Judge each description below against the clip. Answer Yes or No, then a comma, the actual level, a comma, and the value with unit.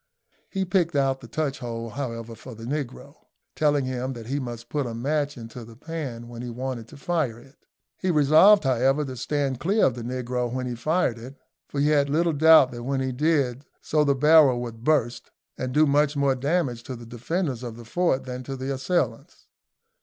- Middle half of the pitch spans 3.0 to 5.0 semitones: Yes, average, 3.7 semitones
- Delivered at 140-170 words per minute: No, fast, 205 wpm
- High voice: No, low, 130 Hz